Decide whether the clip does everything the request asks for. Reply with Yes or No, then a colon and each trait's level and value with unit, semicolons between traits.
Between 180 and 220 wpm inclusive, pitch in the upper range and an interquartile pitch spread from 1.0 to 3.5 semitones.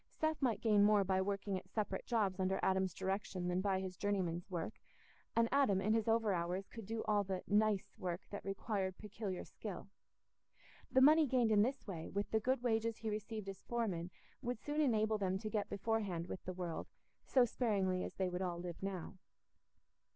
Yes: average, 190 wpm; high, 200 Hz; average, 3.0 semitones